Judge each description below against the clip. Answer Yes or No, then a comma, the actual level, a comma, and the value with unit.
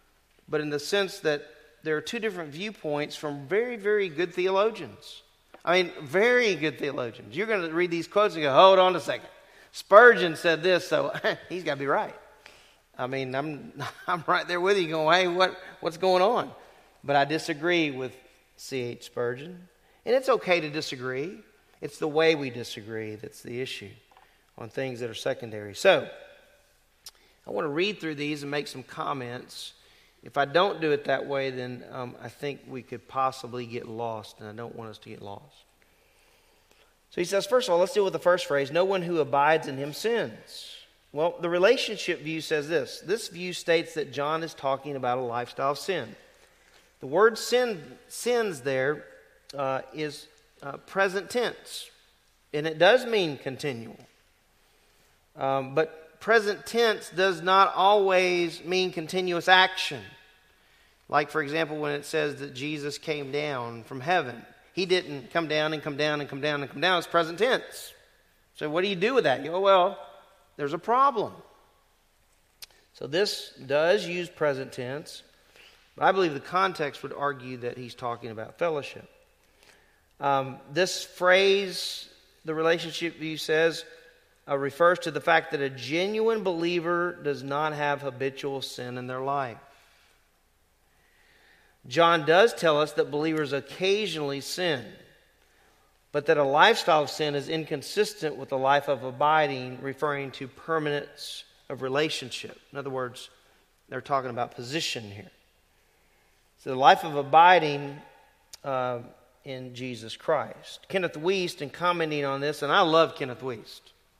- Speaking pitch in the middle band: Yes, medium, 150 Hz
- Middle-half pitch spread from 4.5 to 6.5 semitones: Yes, average, 4.8 semitones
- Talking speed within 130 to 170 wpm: Yes, average, 165 wpm